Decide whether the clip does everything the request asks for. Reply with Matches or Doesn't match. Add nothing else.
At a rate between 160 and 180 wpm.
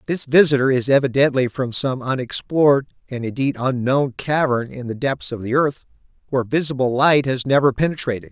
Matches